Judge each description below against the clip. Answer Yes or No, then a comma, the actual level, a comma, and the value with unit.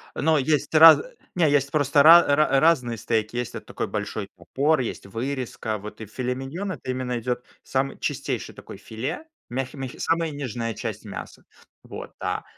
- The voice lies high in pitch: No, low, 130 Hz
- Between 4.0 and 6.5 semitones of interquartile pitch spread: Yes, average, 4.3 semitones